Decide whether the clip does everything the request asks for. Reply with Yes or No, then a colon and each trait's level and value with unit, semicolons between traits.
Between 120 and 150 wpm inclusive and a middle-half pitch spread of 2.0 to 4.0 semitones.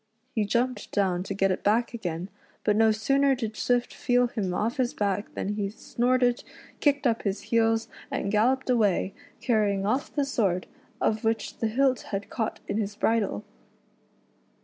No: average, 170 wpm; average, 3.3 semitones